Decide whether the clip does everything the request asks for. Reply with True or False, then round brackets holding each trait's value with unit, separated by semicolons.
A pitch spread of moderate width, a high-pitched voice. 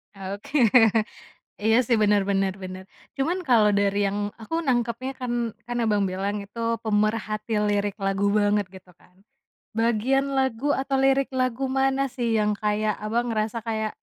True (3.8 semitones; 220 Hz)